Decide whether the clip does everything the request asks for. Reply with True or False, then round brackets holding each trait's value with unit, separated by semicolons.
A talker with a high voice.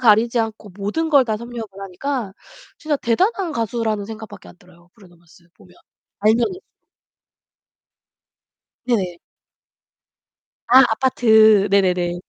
True (220 Hz)